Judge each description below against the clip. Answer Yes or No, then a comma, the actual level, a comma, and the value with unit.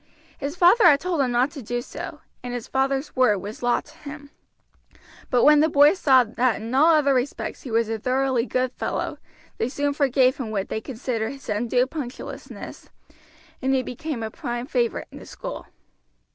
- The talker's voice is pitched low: No, very high, 260 Hz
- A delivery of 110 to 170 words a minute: No, average, 190 wpm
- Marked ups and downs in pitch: No, average, 3.0 semitones